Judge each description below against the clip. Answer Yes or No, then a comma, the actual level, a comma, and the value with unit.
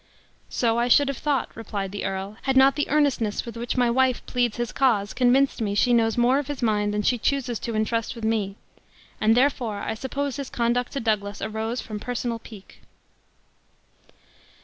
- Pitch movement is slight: No, average, 3.1 semitones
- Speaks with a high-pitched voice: Yes, high, 235 Hz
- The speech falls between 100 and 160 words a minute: No, average, 190 wpm